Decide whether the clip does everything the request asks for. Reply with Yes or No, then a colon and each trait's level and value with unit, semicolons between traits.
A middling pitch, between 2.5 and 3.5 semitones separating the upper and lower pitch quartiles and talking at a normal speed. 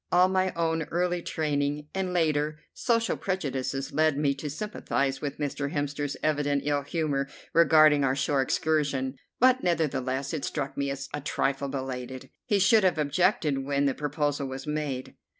Yes: medium, 145 Hz; average, 2.8 semitones; average, 160 wpm